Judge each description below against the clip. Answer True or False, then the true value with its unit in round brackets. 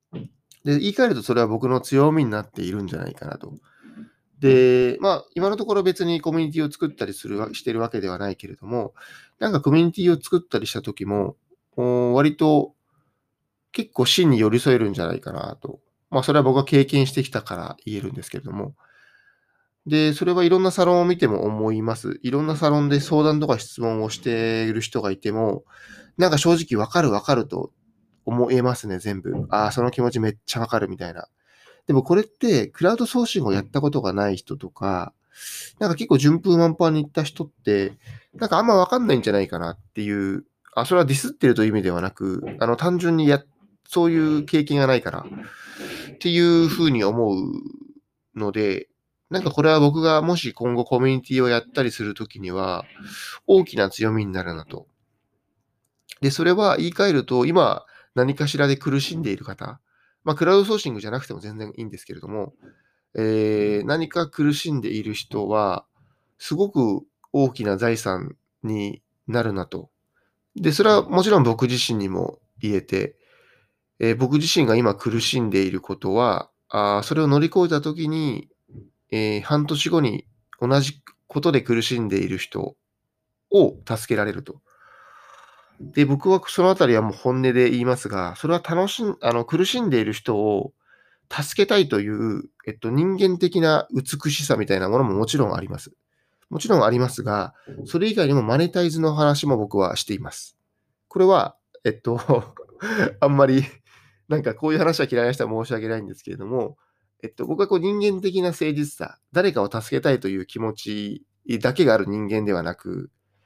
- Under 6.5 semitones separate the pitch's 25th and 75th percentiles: False (6.8 semitones)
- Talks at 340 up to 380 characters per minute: True (355 characters per minute)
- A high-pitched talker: False (135 Hz)